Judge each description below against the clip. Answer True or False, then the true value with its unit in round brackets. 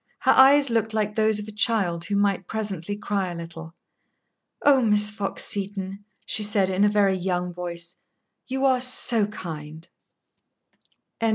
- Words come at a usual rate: True (155 wpm)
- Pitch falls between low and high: False (205 Hz)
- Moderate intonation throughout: True (3.4 semitones)